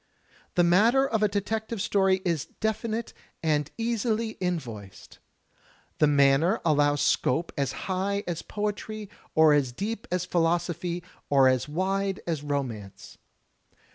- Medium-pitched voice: Yes, medium, 180 Hz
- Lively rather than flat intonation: Yes, wide, 6.0 semitones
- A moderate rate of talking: No, slow, 125 wpm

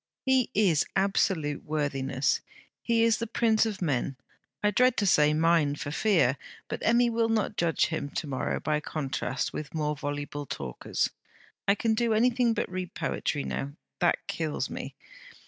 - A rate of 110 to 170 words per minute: Yes, average, 165 wpm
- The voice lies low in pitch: No, medium, 165 Hz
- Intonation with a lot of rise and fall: Yes, wide, 7.1 semitones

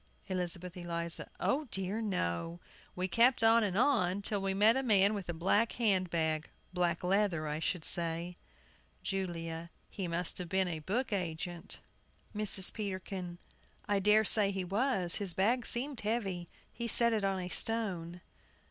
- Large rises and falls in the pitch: No, average, 3.5 semitones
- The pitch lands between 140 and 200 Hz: Yes, high, 190 Hz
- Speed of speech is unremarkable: Yes, average, 160 wpm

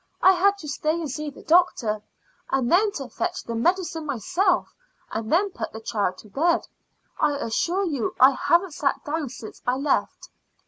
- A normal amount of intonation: No, wide, 6.2 semitones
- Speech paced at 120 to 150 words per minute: No, average, 180 wpm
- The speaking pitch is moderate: No, very high, 300 Hz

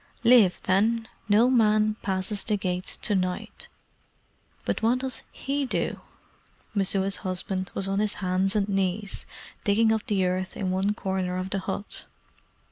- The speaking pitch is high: Yes, high, 195 Hz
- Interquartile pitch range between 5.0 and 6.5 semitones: No, narrow, 2.4 semitones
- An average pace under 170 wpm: Yes, average, 150 wpm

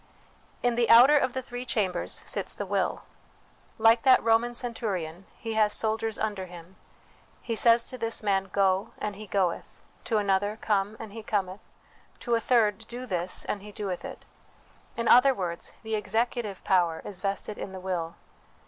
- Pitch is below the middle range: No, high, 210 Hz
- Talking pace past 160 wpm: Yes, average, 175 wpm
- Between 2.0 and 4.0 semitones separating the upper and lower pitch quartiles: Yes, average, 3.2 semitones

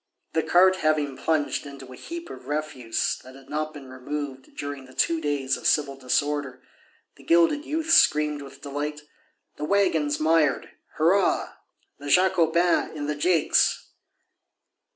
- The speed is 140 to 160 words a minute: Yes, average, 145 wpm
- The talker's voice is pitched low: No, medium, 150 Hz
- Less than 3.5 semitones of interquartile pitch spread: Yes, average, 2.9 semitones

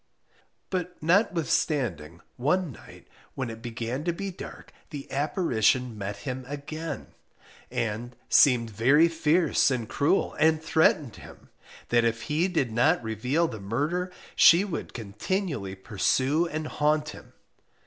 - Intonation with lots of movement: Yes, wide, 6.0 semitones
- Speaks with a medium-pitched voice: Yes, medium, 145 Hz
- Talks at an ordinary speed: No, slow, 130 wpm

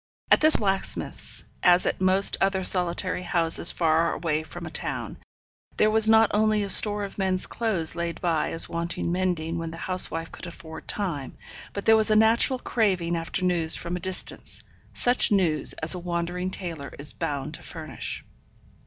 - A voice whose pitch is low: No, medium, 180 Hz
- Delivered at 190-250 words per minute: No, average, 175 wpm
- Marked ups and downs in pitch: No, average, 3.3 semitones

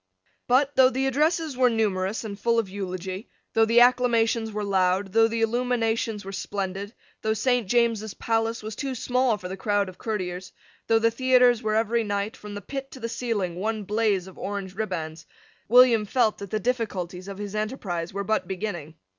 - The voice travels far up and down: No, average, 3.3 semitones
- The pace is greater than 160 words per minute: Yes, average, 190 wpm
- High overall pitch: Yes, high, 220 Hz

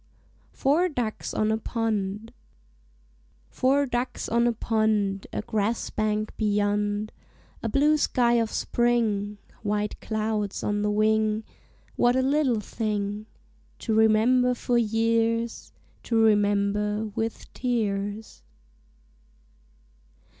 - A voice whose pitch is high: Yes, high, 220 Hz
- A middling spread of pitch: No, narrow, 2.3 semitones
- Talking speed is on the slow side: Yes, slow, 105 wpm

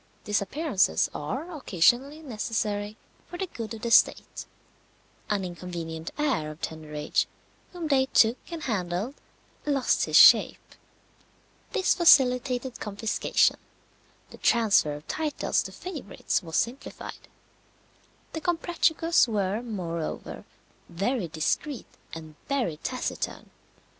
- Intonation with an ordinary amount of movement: No, wide, 8.0 semitones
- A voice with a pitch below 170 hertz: No, high, 225 Hz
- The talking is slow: Yes, slow, 110 wpm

